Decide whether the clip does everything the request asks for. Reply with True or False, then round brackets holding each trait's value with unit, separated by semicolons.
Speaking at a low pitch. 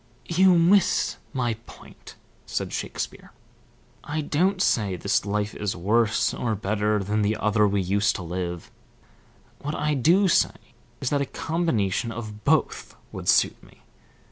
True (110 Hz)